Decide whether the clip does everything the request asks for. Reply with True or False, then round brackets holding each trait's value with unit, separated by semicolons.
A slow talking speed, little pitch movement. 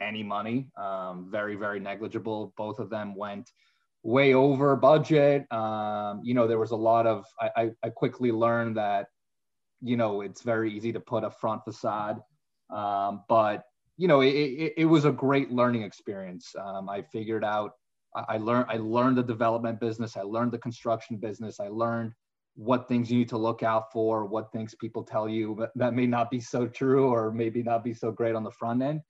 False (200 wpm; 2.3 semitones)